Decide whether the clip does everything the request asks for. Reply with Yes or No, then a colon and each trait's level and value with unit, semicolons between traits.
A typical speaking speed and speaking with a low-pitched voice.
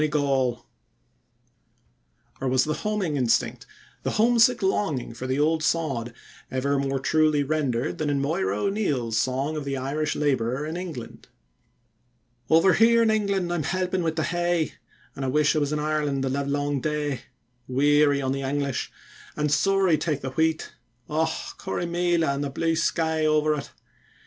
No: average, 165 wpm; medium, 150 Hz